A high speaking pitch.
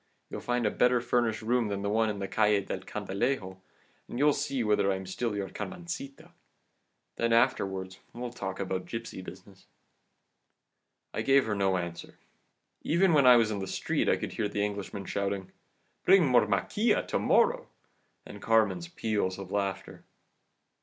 No: low, 110 Hz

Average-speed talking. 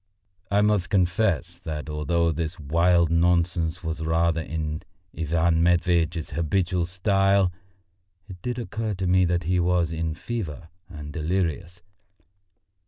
No: slow, 130 wpm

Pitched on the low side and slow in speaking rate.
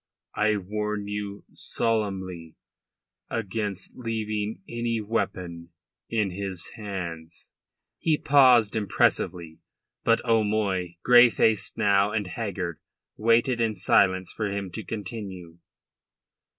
Yes: low, 105 Hz; slow, 100 wpm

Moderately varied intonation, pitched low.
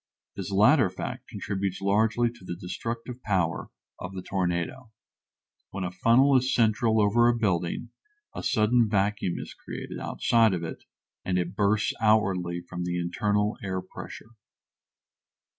Yes: average, 3.9 semitones; low, 100 Hz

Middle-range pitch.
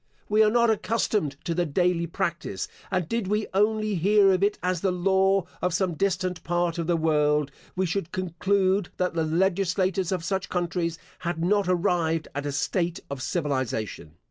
Yes: medium, 180 Hz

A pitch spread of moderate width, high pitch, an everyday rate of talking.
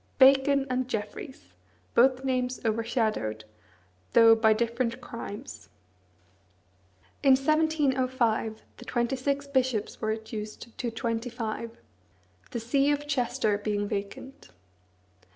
No: average, 3.2 semitones; high, 240 Hz; slow, 105 wpm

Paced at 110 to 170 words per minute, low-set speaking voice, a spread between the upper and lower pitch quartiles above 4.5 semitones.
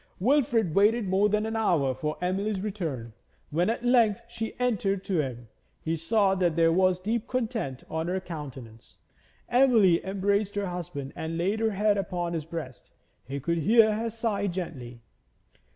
No: average, 165 wpm; high, 190 Hz; average, 4.9 semitones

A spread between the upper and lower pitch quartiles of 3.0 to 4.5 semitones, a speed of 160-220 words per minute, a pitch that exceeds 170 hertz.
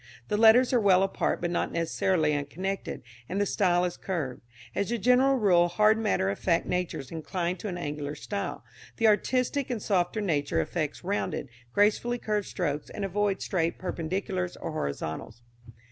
Yes: average, 3.9 semitones; average, 165 wpm; medium, 185 Hz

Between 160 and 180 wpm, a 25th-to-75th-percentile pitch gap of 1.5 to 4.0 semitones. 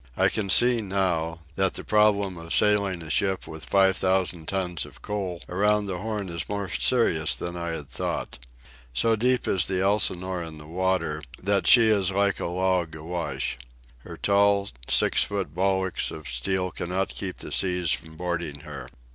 Yes: average, 175 wpm; average, 3.1 semitones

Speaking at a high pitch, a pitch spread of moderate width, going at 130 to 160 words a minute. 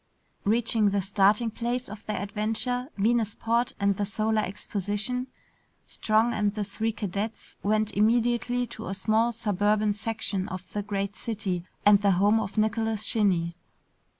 No: high, 215 Hz; narrow, 2.0 semitones; average, 145 wpm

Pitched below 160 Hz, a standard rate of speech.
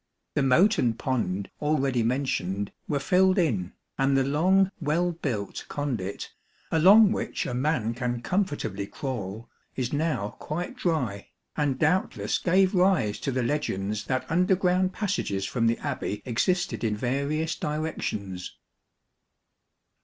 No: medium, 140 Hz; slow, 130 wpm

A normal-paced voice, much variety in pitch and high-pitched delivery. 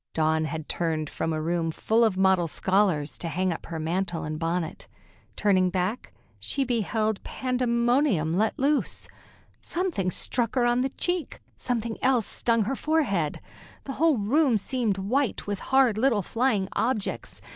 Yes: average, 155 wpm; wide, 6.4 semitones; high, 210 Hz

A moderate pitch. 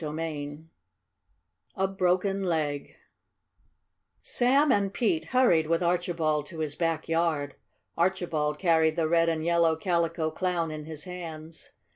Yes: medium, 165 Hz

